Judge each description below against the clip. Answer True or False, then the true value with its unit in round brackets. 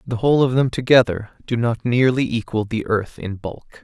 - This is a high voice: False (120 Hz)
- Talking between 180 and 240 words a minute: True (205 wpm)